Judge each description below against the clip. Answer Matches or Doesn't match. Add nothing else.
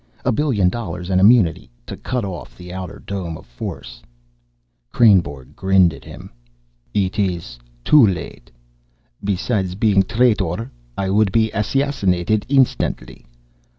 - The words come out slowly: Matches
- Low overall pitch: Matches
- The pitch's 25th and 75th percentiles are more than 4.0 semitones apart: Doesn't match